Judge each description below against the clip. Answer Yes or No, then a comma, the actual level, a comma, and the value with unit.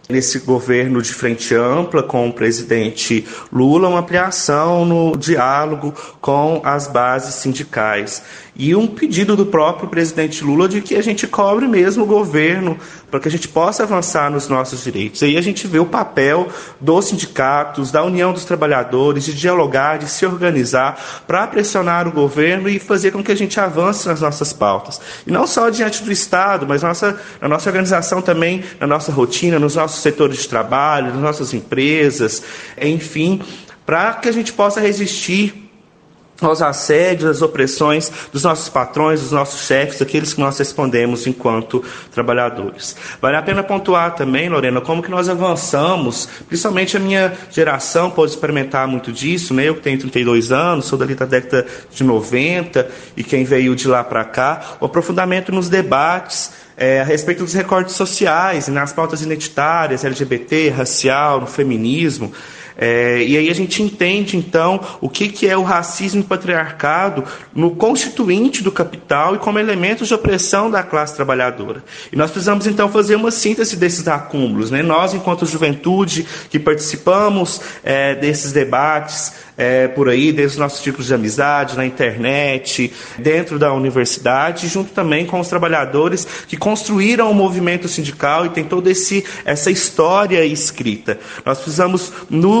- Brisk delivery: No, average, 160 wpm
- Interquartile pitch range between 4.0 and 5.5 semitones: Yes, average, 5.2 semitones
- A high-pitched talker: No, medium, 160 Hz